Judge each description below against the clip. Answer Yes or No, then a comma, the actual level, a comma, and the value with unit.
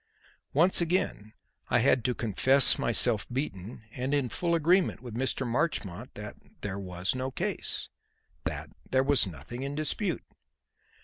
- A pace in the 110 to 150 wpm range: Yes, average, 140 wpm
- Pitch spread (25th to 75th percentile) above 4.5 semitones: Yes, average, 5.0 semitones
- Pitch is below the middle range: Yes, low, 130 Hz